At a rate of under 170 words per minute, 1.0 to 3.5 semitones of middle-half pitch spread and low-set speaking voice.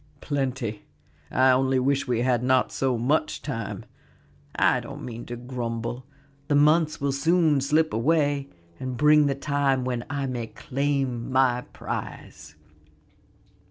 Yes: slow, 135 wpm; average, 2.8 semitones; low, 130 Hz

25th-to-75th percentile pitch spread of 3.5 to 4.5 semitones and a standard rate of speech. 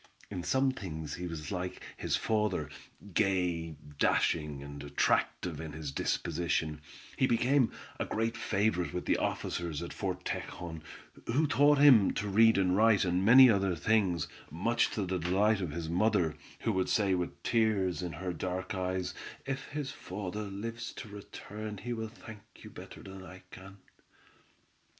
Yes: average, 4.1 semitones; average, 160 wpm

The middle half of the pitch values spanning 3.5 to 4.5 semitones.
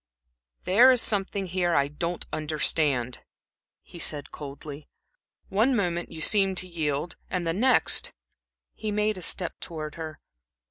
Yes: average, 4.2 semitones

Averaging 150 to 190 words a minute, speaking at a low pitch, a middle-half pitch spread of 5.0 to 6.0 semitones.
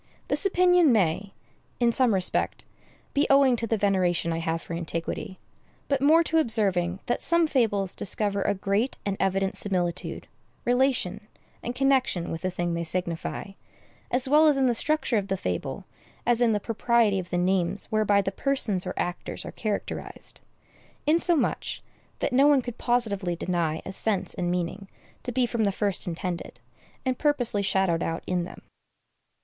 No: average, 165 wpm; high, 205 Hz; wide, 5.5 semitones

